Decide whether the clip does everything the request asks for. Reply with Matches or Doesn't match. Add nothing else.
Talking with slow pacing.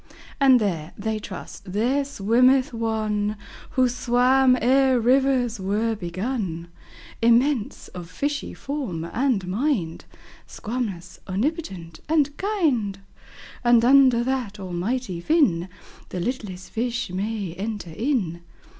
Matches